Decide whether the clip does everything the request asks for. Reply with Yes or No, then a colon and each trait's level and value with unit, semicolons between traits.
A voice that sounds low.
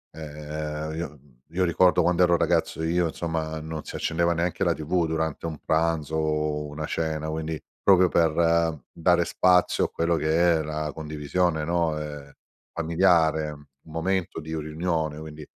Yes: very low, 80 Hz